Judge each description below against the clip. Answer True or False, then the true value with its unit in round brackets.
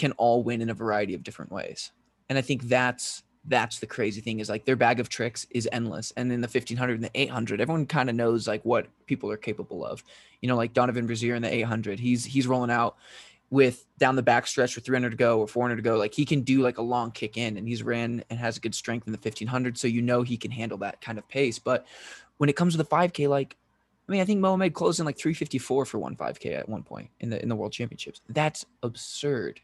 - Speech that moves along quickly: True (260 wpm)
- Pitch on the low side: True (120 Hz)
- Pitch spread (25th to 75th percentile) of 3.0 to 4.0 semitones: False (2.5 semitones)